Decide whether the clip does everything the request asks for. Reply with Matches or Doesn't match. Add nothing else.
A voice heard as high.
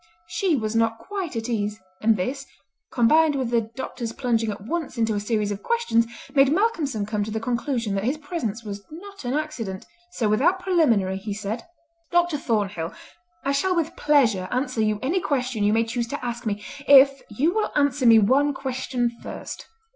Matches